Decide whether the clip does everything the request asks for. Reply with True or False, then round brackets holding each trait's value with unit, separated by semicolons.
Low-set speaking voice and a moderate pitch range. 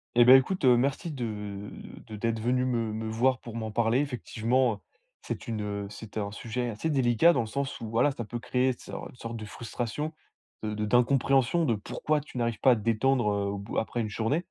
True (120 Hz; 3.2 semitones)